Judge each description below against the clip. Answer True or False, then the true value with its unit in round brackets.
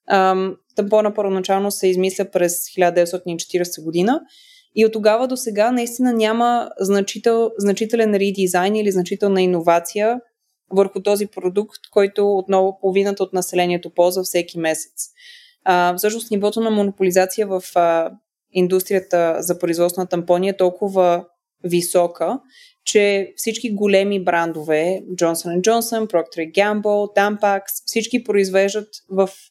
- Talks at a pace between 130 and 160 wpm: False (120 wpm)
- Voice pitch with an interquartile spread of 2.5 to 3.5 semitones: True (3.2 semitones)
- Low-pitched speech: False (195 Hz)